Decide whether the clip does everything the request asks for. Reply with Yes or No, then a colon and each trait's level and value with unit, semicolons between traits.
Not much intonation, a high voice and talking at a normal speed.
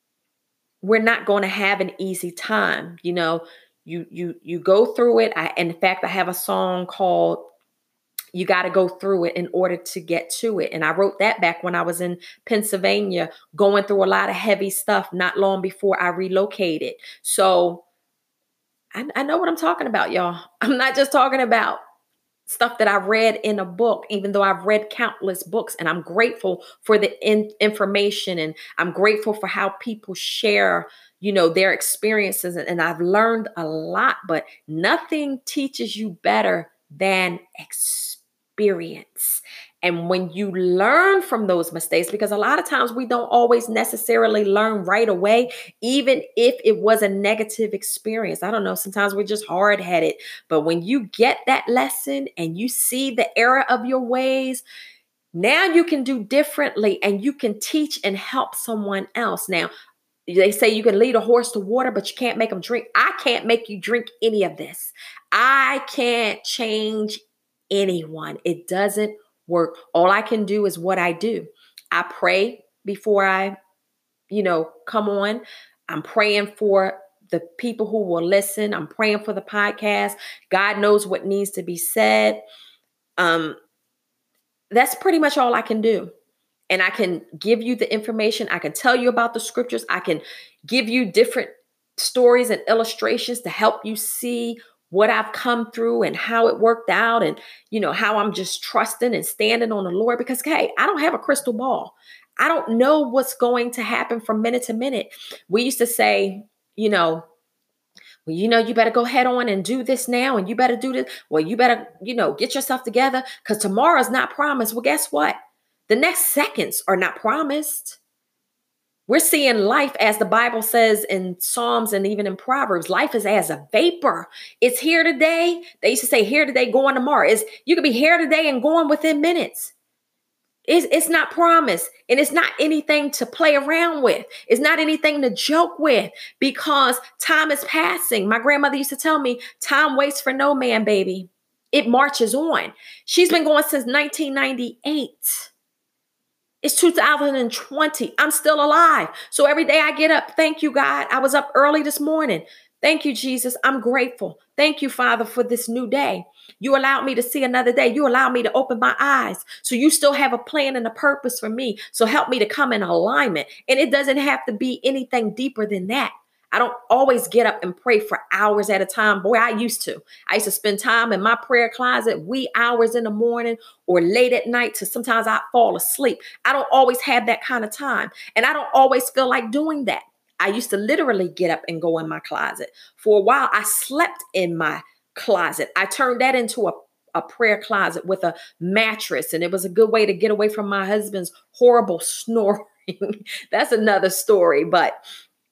No: average, 5.1 semitones; high, 230 Hz; average, 190 wpm